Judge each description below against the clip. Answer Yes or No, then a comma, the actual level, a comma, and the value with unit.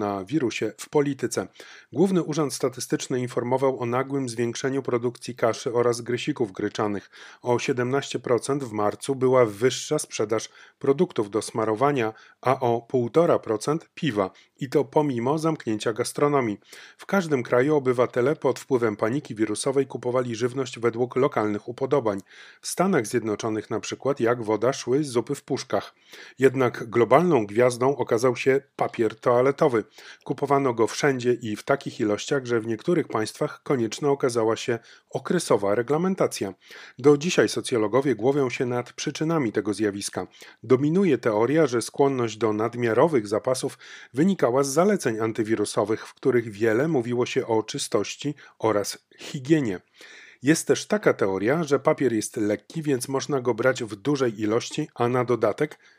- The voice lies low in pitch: Yes, low, 125 Hz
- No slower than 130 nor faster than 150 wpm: Yes, average, 140 wpm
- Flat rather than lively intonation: No, average, 3.6 semitones